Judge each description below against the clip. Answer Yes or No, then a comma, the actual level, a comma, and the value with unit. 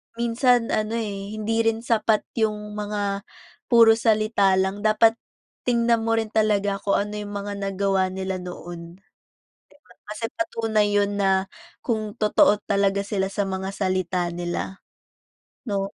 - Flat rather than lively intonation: Yes, narrow, 2.2 semitones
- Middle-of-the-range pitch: No, high, 205 Hz